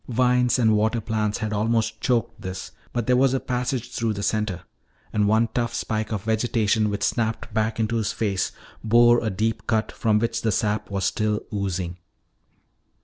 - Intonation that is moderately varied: No, narrow, 1.8 semitones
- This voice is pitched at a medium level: No, low, 110 Hz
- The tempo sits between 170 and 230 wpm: Yes, average, 180 wpm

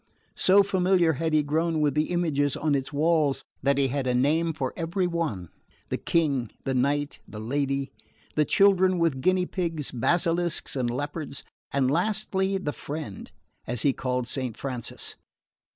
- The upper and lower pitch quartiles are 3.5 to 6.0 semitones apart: Yes, average, 4.0 semitones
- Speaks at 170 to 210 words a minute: No, average, 160 wpm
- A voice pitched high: No, medium, 150 Hz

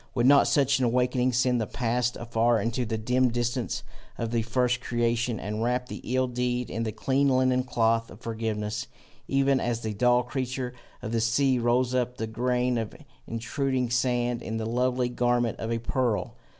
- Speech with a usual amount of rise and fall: No, narrow, 1.6 semitones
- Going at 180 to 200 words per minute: Yes, average, 185 wpm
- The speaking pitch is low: Yes, low, 120 Hz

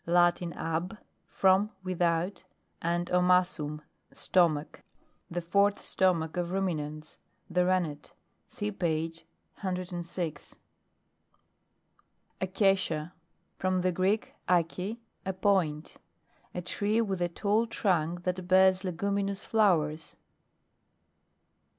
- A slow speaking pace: Yes, slow, 95 wpm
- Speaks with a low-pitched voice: No, medium, 180 Hz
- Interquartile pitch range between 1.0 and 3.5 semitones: Yes, narrow, 2.4 semitones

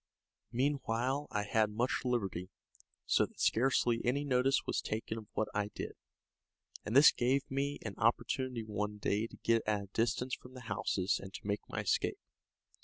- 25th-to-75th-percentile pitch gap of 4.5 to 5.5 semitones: No, average, 3.5 semitones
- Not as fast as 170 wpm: No, average, 175 wpm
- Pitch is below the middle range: Yes, low, 115 Hz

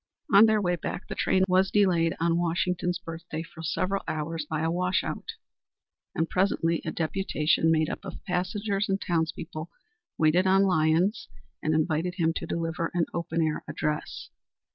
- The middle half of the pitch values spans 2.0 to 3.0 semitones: Yes, narrow, 2.5 semitones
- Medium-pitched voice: Yes, medium, 170 Hz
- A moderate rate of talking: Yes, average, 165 wpm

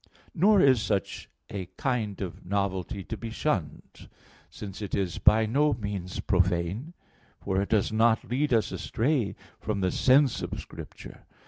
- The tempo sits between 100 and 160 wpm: Yes, average, 150 wpm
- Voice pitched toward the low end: Yes, low, 105 Hz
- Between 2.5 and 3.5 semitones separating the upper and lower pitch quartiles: No, average, 4.5 semitones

